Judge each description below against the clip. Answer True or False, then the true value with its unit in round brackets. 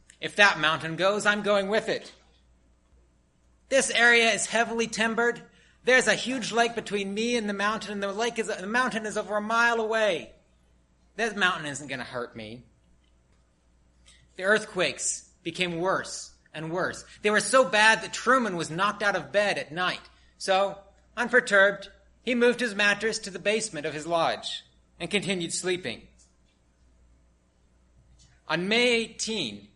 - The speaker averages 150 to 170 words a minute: True (155 wpm)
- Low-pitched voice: False (195 Hz)